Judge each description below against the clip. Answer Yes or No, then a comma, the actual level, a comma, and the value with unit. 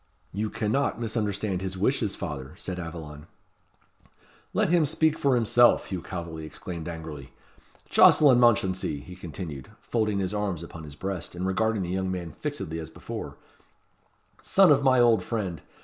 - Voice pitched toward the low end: Yes, very low, 95 Hz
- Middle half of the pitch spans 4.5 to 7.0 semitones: Yes, average, 5.2 semitones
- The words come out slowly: No, average, 150 wpm